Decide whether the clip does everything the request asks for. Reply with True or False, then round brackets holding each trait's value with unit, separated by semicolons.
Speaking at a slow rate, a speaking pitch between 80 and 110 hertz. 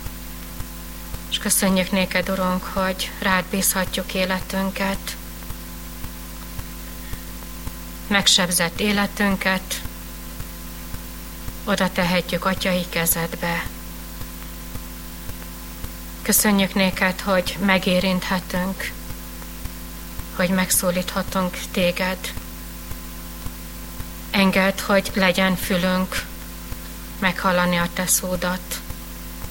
True (60 wpm; 85 Hz)